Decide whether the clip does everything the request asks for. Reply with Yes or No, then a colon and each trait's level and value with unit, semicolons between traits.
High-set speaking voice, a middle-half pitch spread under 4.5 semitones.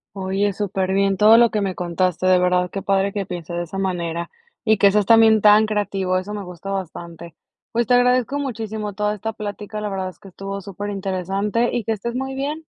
Yes: high, 200 Hz; narrow, 2.6 semitones